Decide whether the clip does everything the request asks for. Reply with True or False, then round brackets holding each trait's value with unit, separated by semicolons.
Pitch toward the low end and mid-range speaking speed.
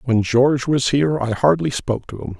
False (130 Hz; 225 wpm)